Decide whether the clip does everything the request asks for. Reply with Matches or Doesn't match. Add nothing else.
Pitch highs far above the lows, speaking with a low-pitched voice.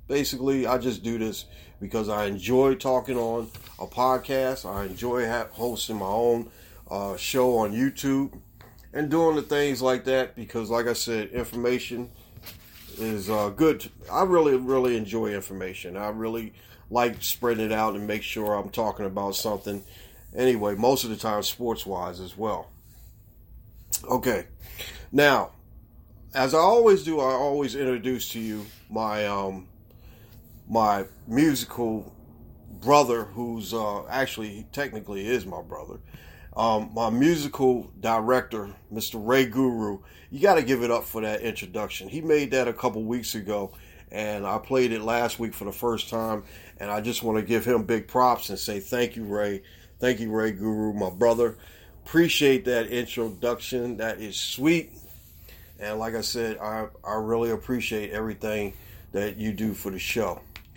Doesn't match